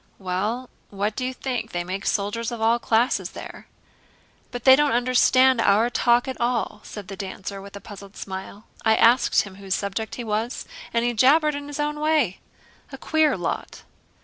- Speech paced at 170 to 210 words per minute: Yes, average, 185 wpm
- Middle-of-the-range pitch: No, high, 230 Hz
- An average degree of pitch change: Yes, average, 4.2 semitones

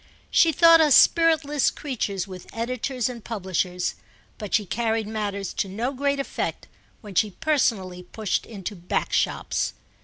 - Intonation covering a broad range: Yes, wide, 5.9 semitones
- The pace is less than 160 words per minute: Yes, average, 145 wpm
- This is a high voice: Yes, high, 220 Hz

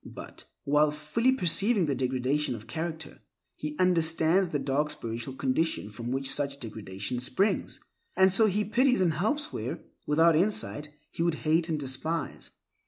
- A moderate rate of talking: Yes, average, 155 wpm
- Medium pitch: Yes, medium, 155 Hz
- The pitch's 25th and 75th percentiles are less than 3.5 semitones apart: No, average, 5.1 semitones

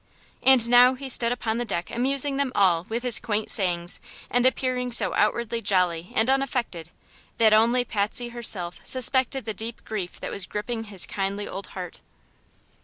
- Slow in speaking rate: No, average, 170 wpm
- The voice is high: Yes, high, 230 Hz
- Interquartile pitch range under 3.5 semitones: No, average, 3.9 semitones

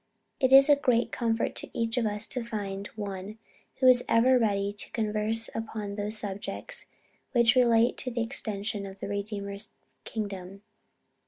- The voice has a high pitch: Yes, high, 215 Hz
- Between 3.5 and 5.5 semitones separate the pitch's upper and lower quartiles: No, average, 2.7 semitones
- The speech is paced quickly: No, average, 160 wpm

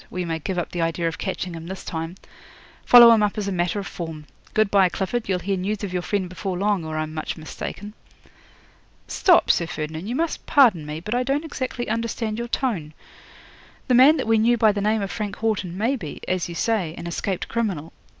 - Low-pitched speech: No, high, 195 Hz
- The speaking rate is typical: No, fast, 220 wpm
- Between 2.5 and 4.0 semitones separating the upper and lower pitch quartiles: No, average, 4.8 semitones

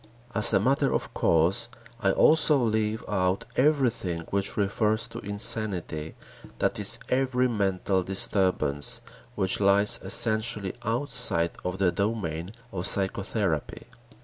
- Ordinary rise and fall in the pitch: Yes, average, 3.4 semitones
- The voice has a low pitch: Yes, low, 100 Hz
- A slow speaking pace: Yes, slow, 120 wpm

